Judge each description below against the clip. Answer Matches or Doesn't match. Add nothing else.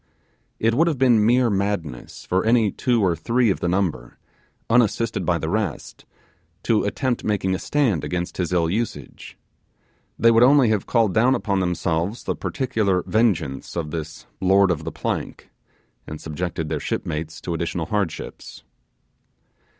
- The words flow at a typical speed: Matches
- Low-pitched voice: Matches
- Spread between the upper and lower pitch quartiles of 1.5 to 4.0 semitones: Doesn't match